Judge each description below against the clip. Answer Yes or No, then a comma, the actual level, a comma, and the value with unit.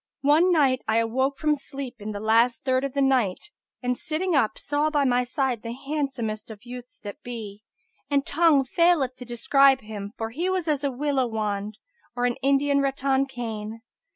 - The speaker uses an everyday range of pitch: Yes, average, 3.8 semitones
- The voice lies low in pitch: No, very high, 260 Hz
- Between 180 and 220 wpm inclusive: Yes, average, 185 wpm